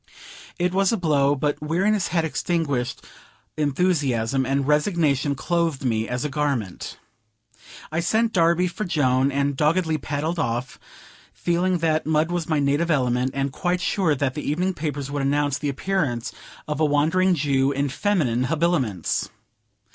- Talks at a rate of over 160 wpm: No, average, 150 wpm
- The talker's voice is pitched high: No, medium, 150 Hz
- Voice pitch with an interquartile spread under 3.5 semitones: No, average, 3.8 semitones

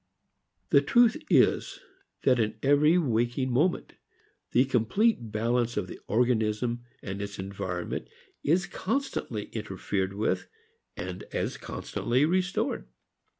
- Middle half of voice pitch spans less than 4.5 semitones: No, wide, 5.6 semitones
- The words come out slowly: Yes, slow, 110 wpm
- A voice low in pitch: Yes, low, 120 Hz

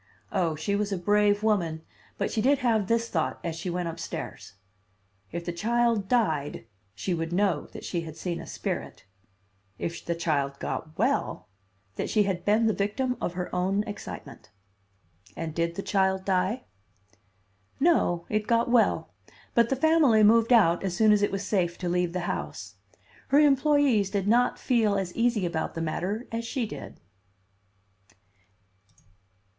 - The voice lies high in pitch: Yes, high, 200 Hz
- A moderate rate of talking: Yes, average, 165 wpm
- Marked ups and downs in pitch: No, average, 4.9 semitones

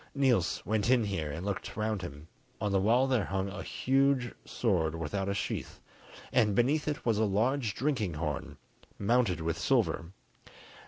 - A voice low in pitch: Yes, low, 105 Hz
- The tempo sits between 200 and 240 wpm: No, average, 165 wpm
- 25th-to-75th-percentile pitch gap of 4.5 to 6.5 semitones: Yes, average, 5.1 semitones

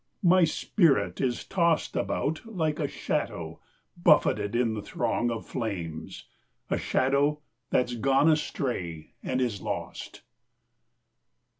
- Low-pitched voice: Yes, low, 130 Hz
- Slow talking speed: Yes, slow, 105 wpm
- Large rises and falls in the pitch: Yes, wide, 5.8 semitones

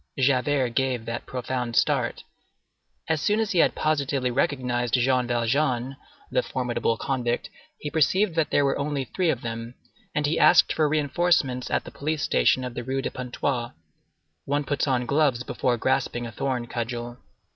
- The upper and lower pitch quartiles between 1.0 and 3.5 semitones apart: Yes, average, 3.1 semitones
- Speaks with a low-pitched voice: Yes, low, 130 Hz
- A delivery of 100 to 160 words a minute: No, average, 170 wpm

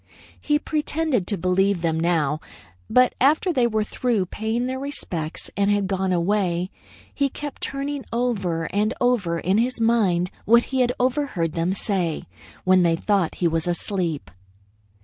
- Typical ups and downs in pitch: No, wide, 6.2 semitones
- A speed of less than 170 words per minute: Yes, average, 155 wpm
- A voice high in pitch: Yes, high, 200 Hz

